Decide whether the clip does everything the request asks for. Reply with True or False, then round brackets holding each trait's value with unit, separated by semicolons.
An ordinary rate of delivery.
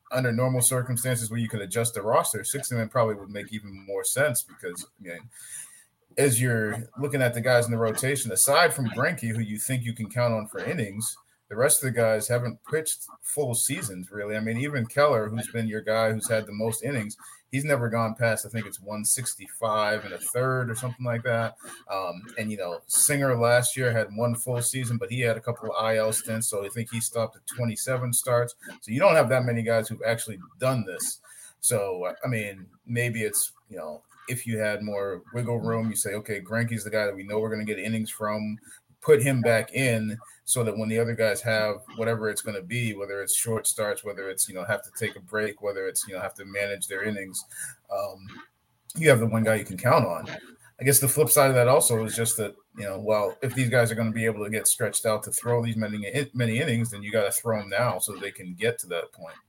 False (245 wpm)